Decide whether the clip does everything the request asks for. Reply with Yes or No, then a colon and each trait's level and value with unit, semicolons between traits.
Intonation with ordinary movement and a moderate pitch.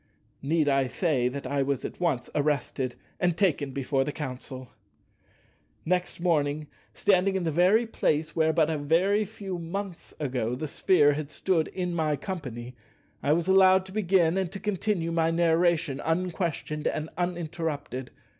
Yes: average, 4.0 semitones; medium, 160 Hz